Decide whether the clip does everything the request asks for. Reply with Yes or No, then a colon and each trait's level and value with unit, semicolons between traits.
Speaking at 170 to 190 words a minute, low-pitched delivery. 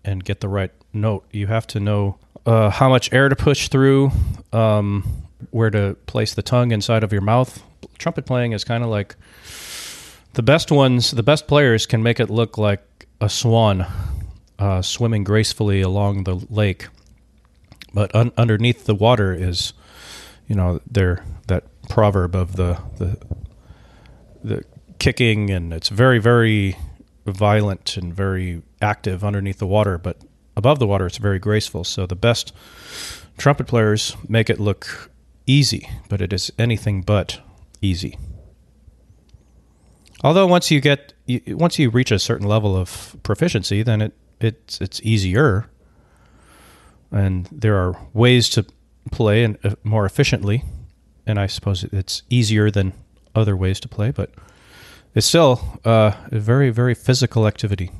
No: average, 150 wpm; low, 105 Hz